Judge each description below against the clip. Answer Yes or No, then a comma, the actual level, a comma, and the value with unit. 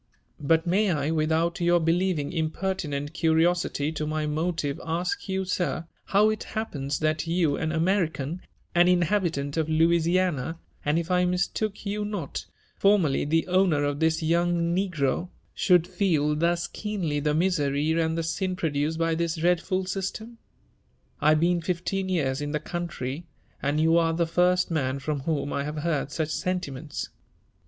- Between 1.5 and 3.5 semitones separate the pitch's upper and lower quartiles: Yes, average, 2.9 semitones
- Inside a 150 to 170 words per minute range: Yes, average, 165 wpm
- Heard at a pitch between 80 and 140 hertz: No, medium, 165 Hz